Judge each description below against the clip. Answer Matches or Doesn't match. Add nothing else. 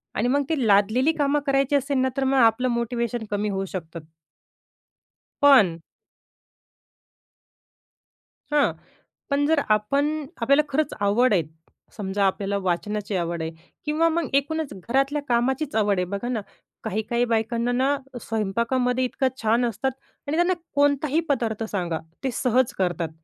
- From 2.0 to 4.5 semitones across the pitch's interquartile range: Doesn't match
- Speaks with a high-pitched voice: Matches